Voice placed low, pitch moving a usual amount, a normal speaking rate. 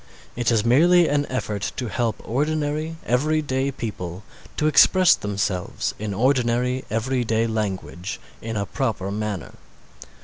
No: low, 120 Hz; average, 5.0 semitones; slow, 125 wpm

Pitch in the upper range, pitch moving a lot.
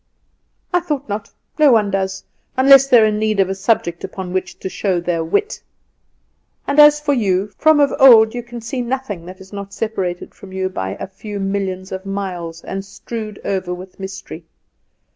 No: high, 200 Hz; average, 4.2 semitones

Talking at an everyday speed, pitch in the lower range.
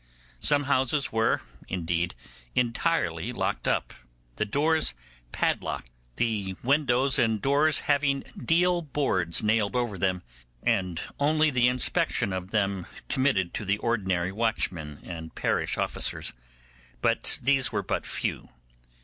No: slow, 125 wpm; low, 115 Hz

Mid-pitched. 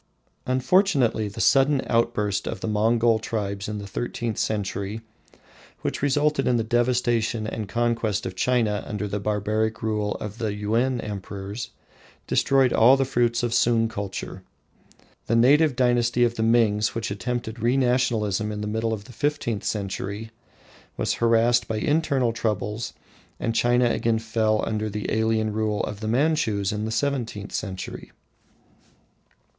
No: low, 115 Hz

